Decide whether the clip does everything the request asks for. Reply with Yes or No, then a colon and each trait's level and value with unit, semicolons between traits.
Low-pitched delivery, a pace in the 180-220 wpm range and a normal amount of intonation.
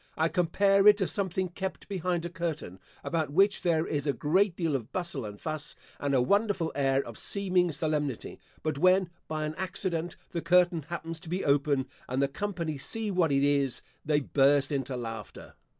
No: medium, 160 Hz; average, 185 wpm; average, 4.3 semitones